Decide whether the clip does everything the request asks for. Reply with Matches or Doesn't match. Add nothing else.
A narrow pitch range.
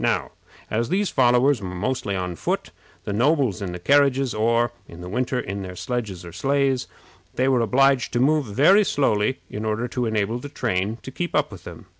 Doesn't match